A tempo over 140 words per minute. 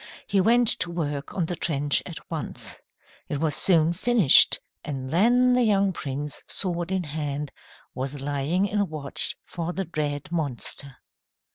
Yes: average, 150 wpm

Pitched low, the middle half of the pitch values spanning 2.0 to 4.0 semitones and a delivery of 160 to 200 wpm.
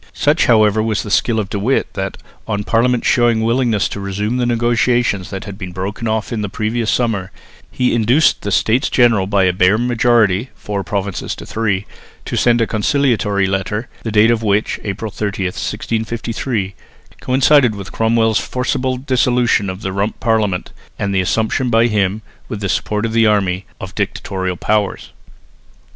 Yes: low, 110 Hz; average, 3.0 semitones; average, 175 wpm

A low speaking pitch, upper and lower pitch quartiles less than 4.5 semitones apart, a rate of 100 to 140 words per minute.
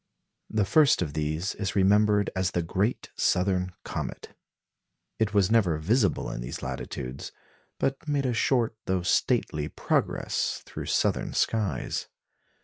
Yes: low, 100 Hz; average, 4.1 semitones; slow, 135 wpm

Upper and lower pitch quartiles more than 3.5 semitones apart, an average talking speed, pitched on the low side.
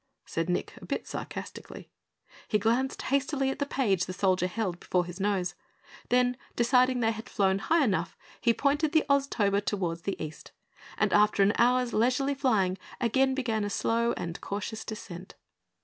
No: average, 5.2 semitones; average, 165 wpm; high, 220 Hz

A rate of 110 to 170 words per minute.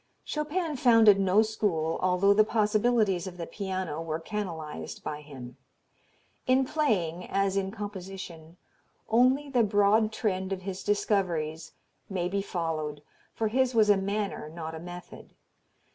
Yes: average, 140 wpm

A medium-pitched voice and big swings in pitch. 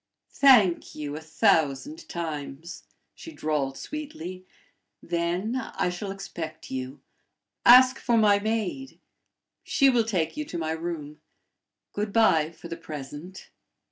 Yes: medium, 175 Hz; wide, 6.3 semitones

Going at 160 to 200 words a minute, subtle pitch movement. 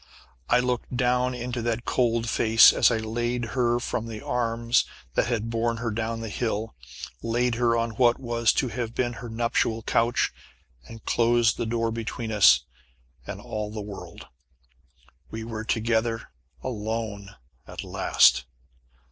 No: average, 150 wpm; narrow, 1.2 semitones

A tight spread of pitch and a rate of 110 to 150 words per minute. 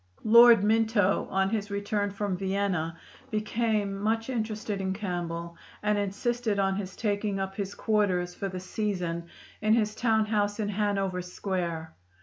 Yes: narrow, 2.1 semitones; average, 145 wpm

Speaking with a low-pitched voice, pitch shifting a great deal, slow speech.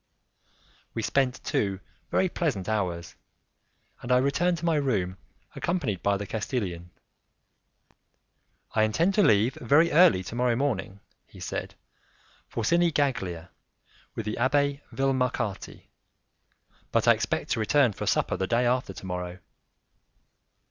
Yes: low, 120 Hz; wide, 6.4 semitones; slow, 130 wpm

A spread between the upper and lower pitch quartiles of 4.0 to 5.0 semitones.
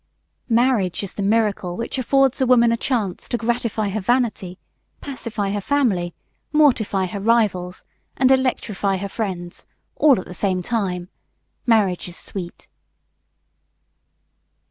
Yes: average, 4.4 semitones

